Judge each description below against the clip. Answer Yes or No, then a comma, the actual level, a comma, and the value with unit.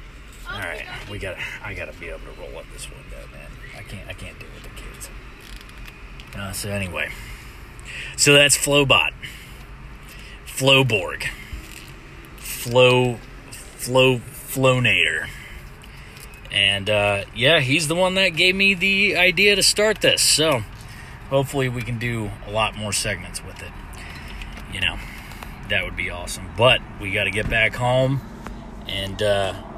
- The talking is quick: No, average, 140 wpm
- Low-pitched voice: Yes, low, 115 Hz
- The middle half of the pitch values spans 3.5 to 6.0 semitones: Yes, average, 5.0 semitones